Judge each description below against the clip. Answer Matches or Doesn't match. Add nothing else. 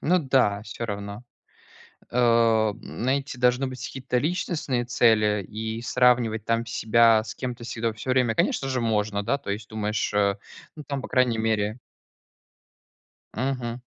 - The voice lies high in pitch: Doesn't match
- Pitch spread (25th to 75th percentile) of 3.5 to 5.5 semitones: Doesn't match